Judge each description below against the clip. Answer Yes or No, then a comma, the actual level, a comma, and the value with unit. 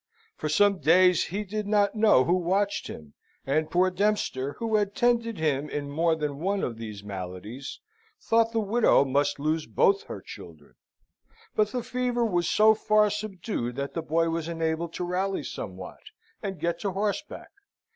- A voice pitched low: No, medium, 175 Hz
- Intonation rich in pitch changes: Yes, wide, 6.4 semitones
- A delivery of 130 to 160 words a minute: No, average, 170 wpm